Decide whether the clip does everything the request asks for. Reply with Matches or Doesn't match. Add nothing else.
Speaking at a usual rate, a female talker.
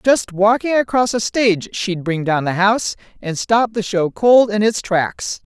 Matches